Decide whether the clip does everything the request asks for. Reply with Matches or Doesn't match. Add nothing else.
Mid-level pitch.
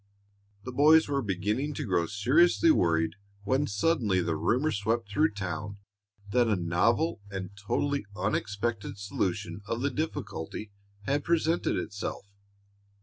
Doesn't match